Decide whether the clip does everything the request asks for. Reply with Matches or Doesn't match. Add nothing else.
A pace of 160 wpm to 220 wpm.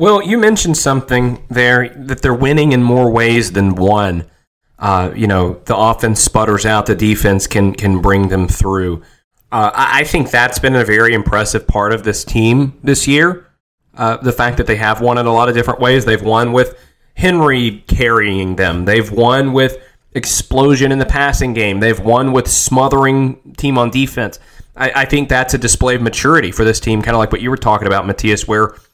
Matches